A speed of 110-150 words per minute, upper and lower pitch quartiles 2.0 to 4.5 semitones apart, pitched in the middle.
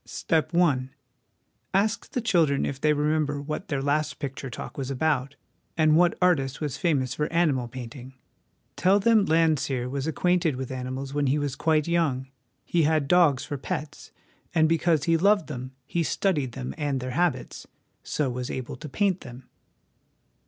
No: average, 170 wpm; average, 3.9 semitones; medium, 150 Hz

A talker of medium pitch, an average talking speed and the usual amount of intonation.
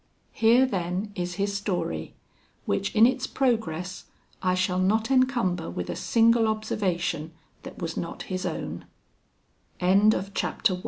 No: high, 195 Hz; average, 145 wpm; average, 3.8 semitones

